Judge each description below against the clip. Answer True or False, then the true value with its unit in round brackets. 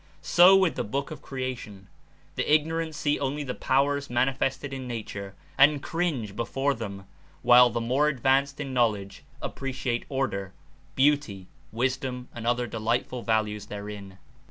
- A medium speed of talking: True (155 wpm)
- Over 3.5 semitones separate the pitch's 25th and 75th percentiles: True (4.0 semitones)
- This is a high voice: False (130 Hz)